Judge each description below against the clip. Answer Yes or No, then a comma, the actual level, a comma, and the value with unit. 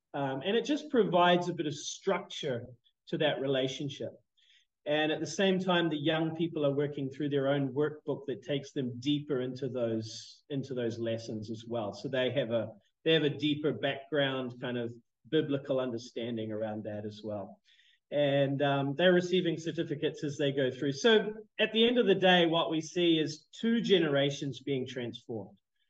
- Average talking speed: Yes, average, 180 wpm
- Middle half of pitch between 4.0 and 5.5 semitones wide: Yes, average, 4.4 semitones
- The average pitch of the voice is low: No, medium, 145 Hz